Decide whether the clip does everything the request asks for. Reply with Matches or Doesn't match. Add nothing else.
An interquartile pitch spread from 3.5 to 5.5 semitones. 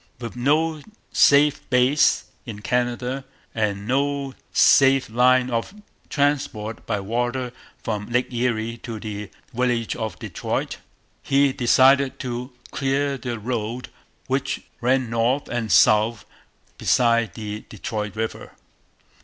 Doesn't match